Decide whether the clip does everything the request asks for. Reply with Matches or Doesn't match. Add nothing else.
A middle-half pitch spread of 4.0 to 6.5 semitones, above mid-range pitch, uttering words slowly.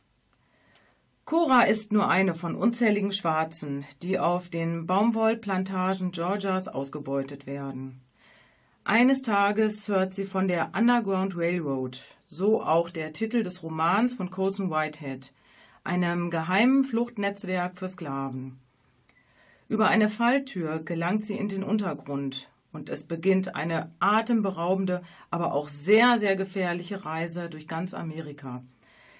Doesn't match